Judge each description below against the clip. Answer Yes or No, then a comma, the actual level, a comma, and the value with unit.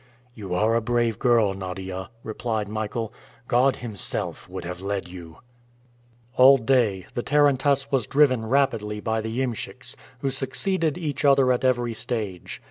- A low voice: Yes, low, 115 Hz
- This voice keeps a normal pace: Yes, average, 145 wpm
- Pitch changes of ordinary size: Yes, average, 4.2 semitones